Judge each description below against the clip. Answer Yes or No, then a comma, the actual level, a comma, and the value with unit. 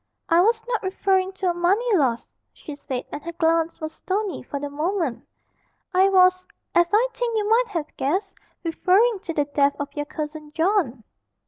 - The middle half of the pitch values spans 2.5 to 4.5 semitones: No, average, 5.0 semitones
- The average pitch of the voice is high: Yes, very high, 345 Hz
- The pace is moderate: Yes, average, 185 wpm